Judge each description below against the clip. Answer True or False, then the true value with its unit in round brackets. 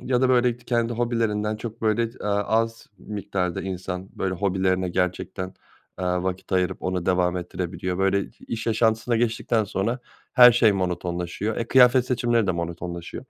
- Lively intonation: False (4.2 semitones)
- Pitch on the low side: True (100 Hz)